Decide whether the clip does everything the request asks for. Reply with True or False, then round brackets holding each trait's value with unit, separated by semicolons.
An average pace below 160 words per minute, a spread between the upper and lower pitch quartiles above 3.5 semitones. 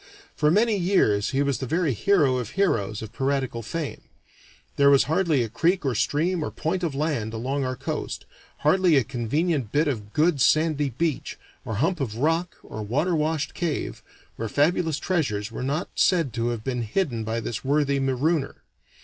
False (180 wpm; 5.4 semitones)